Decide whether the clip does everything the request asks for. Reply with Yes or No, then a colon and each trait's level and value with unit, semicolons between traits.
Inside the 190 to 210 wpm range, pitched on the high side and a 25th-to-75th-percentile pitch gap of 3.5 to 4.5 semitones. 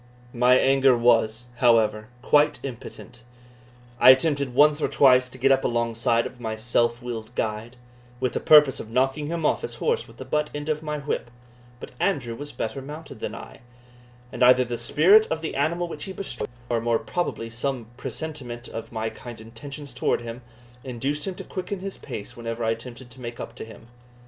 No: average, 195 wpm; low, 125 Hz; average, 4.0 semitones